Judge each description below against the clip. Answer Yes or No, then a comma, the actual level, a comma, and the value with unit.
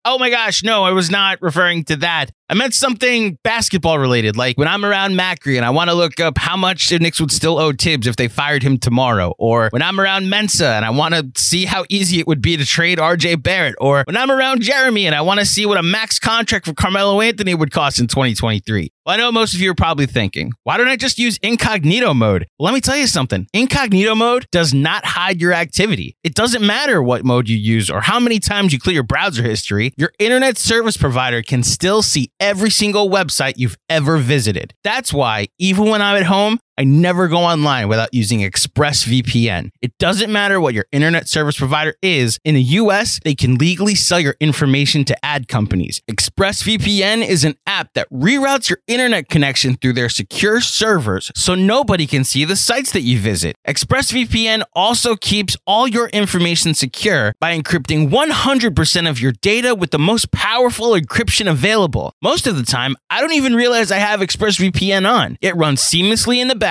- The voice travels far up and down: Yes, wide, 7.5 semitones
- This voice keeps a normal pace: No, fast, 210 wpm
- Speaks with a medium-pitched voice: Yes, medium, 170 Hz